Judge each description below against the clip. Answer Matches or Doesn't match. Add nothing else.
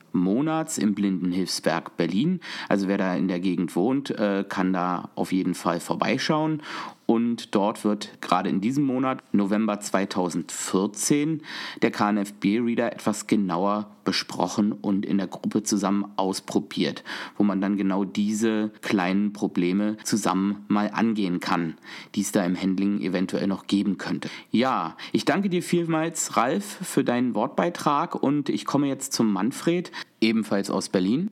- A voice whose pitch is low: Matches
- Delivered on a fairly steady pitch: Doesn't match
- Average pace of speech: Matches